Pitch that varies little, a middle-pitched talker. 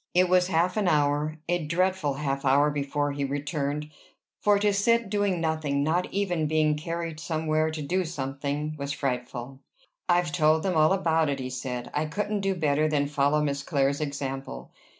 No: average, 3.7 semitones; medium, 155 Hz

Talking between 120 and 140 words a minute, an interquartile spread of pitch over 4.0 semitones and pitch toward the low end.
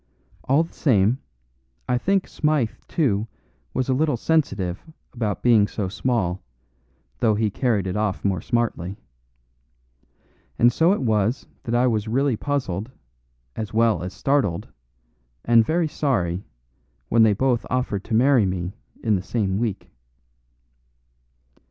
Yes: slow, 135 wpm; average, 4.6 semitones; low, 115 Hz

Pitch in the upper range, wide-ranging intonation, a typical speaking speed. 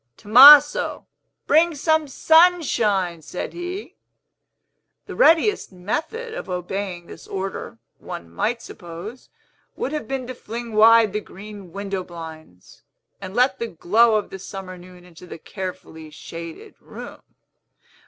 No: high, 205 Hz; wide, 6.6 semitones; slow, 130 wpm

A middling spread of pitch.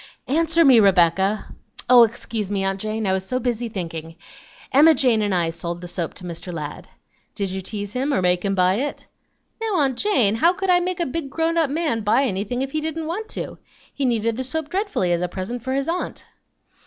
No: wide, 7.8 semitones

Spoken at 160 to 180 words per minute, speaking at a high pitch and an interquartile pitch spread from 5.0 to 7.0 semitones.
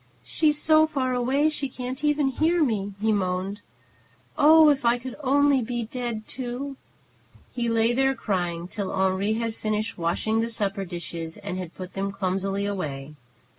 Yes: average, 165 wpm; high, 225 Hz; wide, 5.6 semitones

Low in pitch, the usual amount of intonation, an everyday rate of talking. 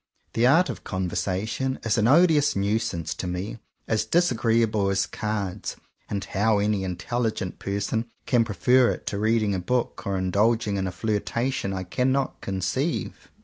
Yes: low, 105 Hz; average, 3.5 semitones; average, 160 wpm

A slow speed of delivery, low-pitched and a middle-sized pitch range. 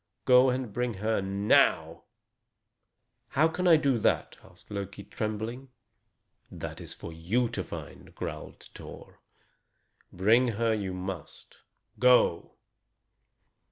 Yes: slow, 115 wpm; low, 110 Hz; average, 4.4 semitones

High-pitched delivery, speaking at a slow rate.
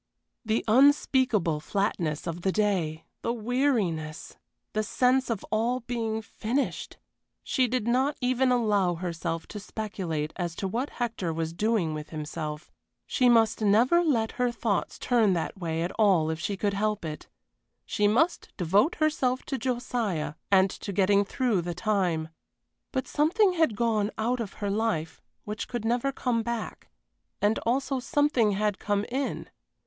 No: high, 215 Hz; average, 155 wpm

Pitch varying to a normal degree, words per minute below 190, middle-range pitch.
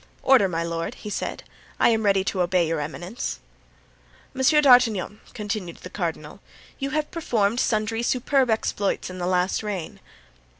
No: average, 4.7 semitones; average, 145 wpm; high, 205 Hz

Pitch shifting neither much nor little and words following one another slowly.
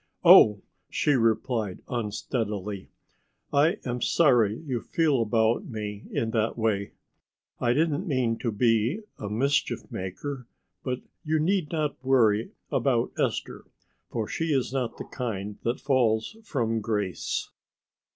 Yes: average, 4.3 semitones; slow, 130 wpm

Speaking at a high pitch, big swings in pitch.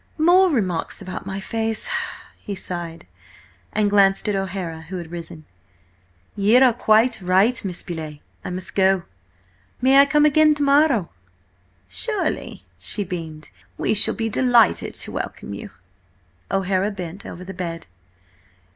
No: high, 195 Hz; average, 4.7 semitones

